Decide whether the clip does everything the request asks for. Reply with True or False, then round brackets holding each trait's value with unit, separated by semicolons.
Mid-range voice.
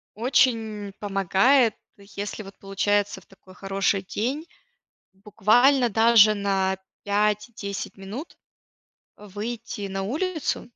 False (205 Hz)